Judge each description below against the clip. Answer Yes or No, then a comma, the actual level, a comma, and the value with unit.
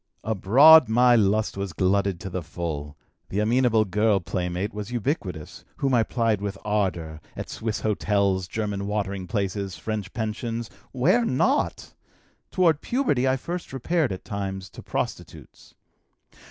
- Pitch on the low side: Yes, low, 105 Hz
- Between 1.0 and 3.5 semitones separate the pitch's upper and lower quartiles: No, average, 4.0 semitones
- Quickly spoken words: No, average, 140 wpm